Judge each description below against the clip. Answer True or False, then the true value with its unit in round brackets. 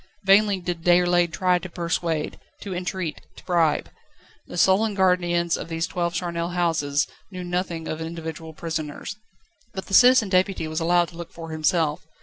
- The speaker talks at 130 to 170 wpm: True (160 wpm)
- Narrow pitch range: True (2.0 semitones)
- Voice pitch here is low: False (175 Hz)